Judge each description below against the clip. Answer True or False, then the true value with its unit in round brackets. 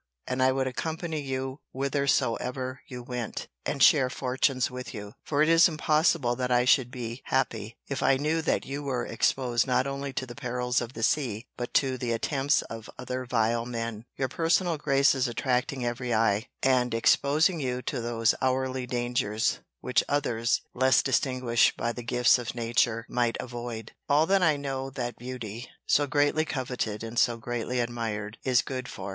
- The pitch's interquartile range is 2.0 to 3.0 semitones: True (2.5 semitones)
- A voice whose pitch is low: True (125 Hz)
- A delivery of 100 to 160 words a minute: False (175 wpm)